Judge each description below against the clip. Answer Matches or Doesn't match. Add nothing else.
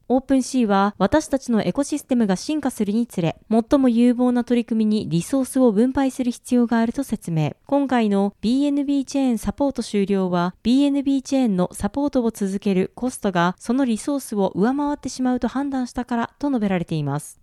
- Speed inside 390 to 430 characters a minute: Matches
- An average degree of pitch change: Matches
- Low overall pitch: Doesn't match